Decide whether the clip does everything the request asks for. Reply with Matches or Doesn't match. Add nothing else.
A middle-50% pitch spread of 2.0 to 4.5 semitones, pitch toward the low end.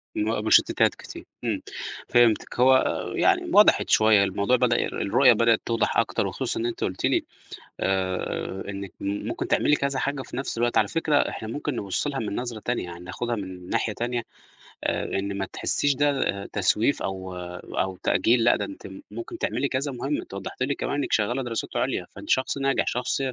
Doesn't match